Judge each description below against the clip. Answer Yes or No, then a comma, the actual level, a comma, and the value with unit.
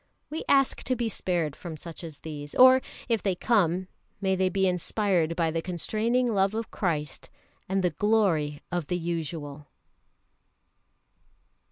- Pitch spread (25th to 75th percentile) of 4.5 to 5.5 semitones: Yes, average, 4.8 semitones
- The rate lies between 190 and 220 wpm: No, average, 150 wpm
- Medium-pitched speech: Yes, medium, 180 Hz